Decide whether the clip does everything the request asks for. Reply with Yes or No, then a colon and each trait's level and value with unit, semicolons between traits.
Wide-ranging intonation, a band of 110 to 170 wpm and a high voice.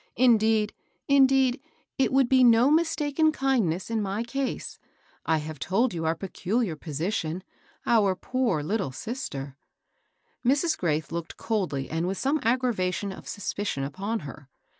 Yes: wide, 7.5 semitones; average, 160 wpm; high, 210 Hz